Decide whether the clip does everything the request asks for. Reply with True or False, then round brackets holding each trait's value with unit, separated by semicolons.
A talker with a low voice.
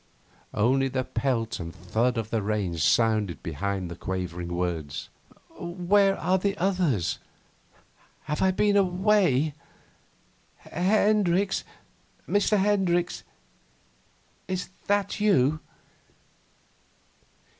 False (150 Hz)